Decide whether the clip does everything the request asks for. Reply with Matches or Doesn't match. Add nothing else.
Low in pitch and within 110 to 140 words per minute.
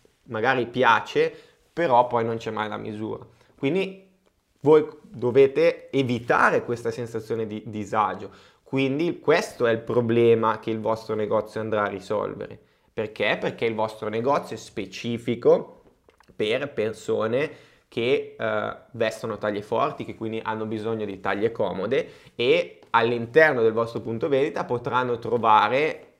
Matches